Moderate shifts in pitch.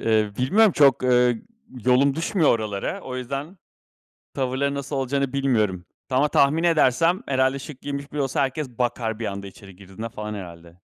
Yes: average, 4.3 semitones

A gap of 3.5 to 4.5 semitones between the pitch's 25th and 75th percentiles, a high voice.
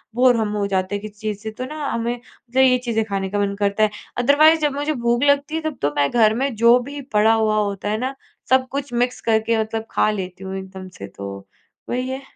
Yes: average, 4.1 semitones; high, 225 Hz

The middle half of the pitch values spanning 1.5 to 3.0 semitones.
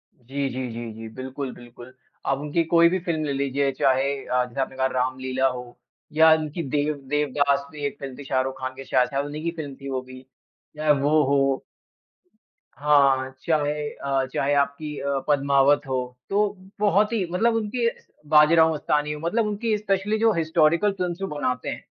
No: average, 3.4 semitones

